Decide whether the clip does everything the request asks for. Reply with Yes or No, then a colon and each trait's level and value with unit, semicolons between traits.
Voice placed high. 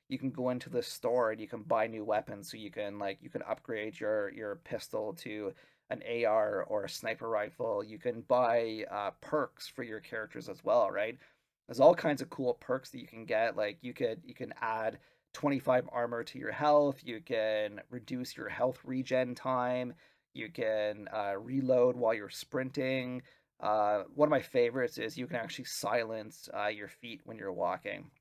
No: low, 125 Hz